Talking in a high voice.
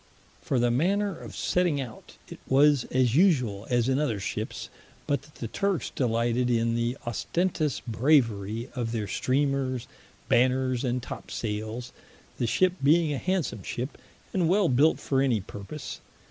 No: low, 130 Hz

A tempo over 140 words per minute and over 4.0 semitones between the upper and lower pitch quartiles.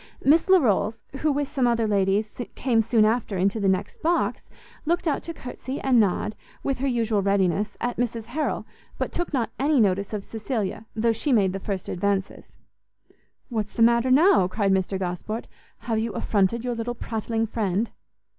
No: average, 175 wpm; average, 3.7 semitones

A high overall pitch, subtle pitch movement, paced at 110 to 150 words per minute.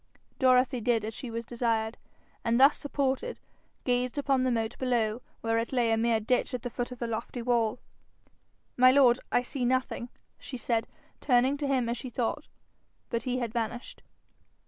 No: high, 245 Hz; narrow, 1.8 semitones; average, 180 wpm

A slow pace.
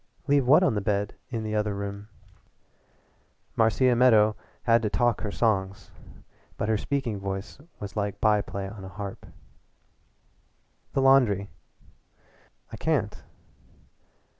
Yes: slow, 125 wpm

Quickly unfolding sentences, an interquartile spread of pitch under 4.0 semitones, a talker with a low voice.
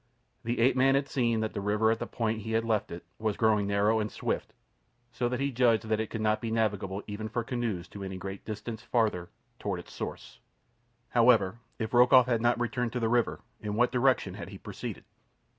Yes: fast, 215 wpm; narrow, 2.4 semitones; low, 110 Hz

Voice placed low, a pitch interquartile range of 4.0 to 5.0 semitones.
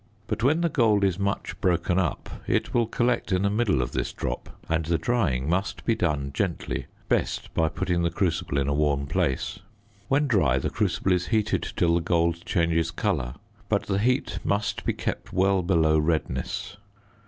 Yes: very low, 90 Hz; average, 4.3 semitones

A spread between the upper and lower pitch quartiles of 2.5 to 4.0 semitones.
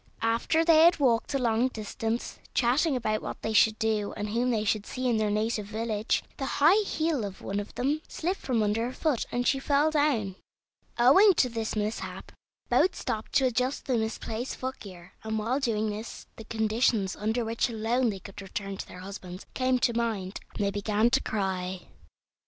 Yes: average, 3.4 semitones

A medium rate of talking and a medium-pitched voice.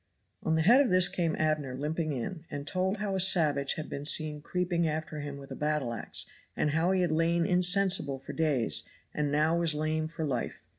No: fast, 210 wpm; medium, 155 Hz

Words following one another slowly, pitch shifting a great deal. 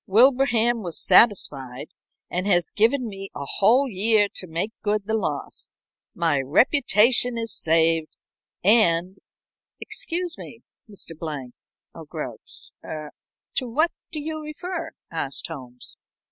Yes: slow, 130 wpm; wide, 7.0 semitones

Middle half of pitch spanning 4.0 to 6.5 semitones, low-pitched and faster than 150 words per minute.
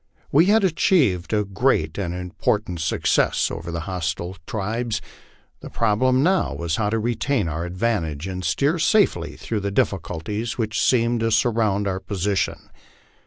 Yes: average, 4.7 semitones; low, 105 Hz; average, 160 wpm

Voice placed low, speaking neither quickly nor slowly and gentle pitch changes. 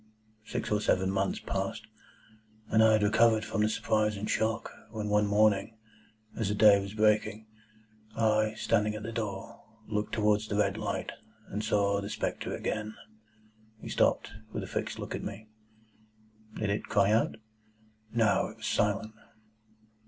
Yes: low, 105 Hz; average, 160 wpm; narrow, 1.1 semitones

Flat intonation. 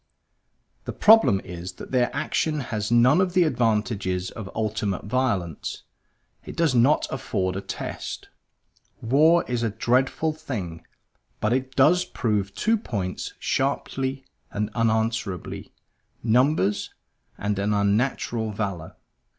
No: average, 4.9 semitones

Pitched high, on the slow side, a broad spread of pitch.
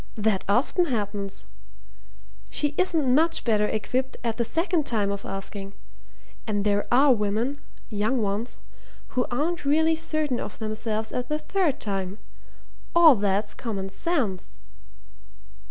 Yes: high, 230 Hz; slow, 130 wpm; wide, 6.2 semitones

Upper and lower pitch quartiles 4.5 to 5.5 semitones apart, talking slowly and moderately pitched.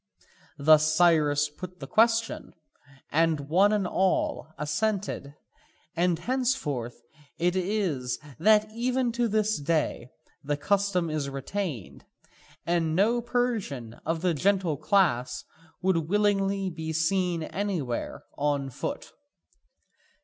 Yes: average, 5.2 semitones; slow, 110 wpm; medium, 175 Hz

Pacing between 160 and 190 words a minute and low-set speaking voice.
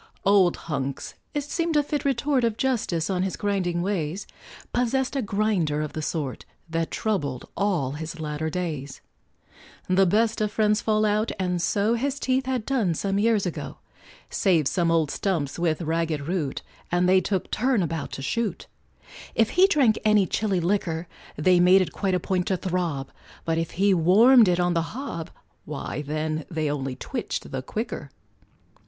No: average, 170 wpm; medium, 185 Hz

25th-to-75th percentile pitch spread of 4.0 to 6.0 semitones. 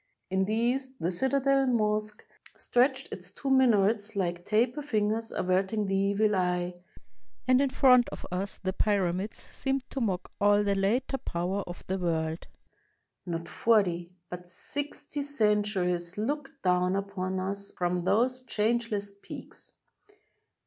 Yes: average, 5.0 semitones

